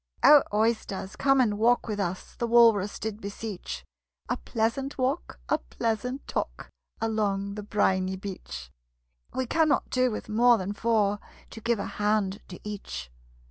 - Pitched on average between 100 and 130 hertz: No, high, 215 Hz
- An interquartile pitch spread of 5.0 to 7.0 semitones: No, average, 3.1 semitones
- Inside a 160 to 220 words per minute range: No, average, 150 wpm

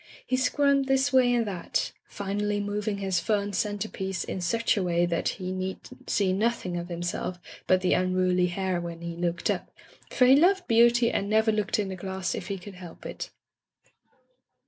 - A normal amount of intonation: Yes, average, 3.7 semitones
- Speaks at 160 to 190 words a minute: Yes, average, 185 wpm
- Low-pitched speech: No, high, 195 Hz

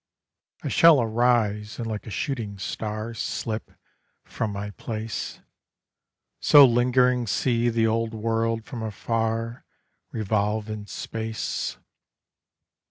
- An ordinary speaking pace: No, slow, 105 wpm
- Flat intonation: Yes, narrow, 1.6 semitones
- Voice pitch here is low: Yes, low, 115 Hz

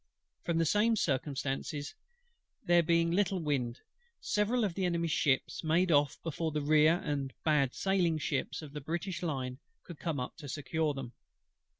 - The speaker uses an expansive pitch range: No, average, 3.4 semitones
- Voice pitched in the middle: Yes, medium, 155 Hz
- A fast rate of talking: No, average, 175 wpm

